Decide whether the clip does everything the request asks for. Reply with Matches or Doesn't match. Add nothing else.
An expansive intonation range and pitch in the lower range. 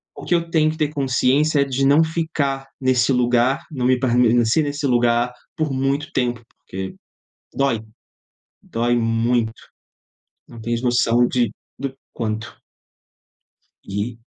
Doesn't match